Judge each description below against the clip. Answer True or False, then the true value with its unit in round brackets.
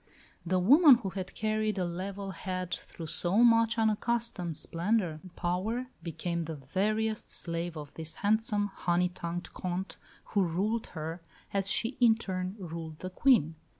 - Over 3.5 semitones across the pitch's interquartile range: True (4.2 semitones)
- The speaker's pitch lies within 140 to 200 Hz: True (185 Hz)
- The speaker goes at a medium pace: True (150 wpm)